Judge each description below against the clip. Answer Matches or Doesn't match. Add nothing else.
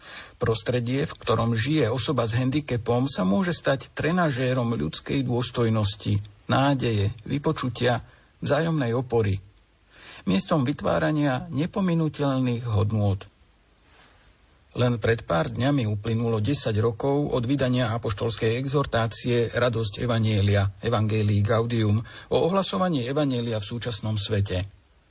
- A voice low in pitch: Matches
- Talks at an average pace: Doesn't match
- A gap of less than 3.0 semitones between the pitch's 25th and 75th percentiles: Doesn't match